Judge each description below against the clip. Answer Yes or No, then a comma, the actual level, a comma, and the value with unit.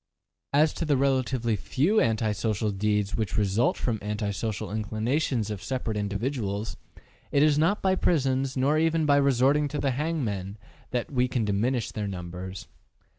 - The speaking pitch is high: No, low, 120 Hz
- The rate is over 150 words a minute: Yes, average, 160 wpm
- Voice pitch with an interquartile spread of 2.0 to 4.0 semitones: No, average, 5.2 semitones